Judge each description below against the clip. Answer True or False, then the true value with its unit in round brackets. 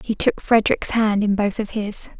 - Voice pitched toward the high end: True (210 Hz)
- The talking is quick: True (220 wpm)